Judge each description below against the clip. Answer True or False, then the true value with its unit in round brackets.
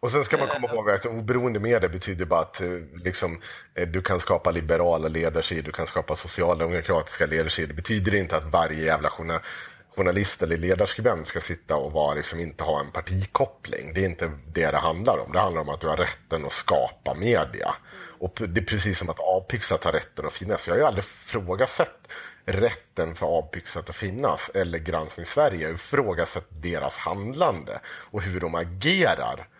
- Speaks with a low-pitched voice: True (90 Hz)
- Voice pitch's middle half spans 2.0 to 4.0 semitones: True (2.8 semitones)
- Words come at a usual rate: True (180 wpm)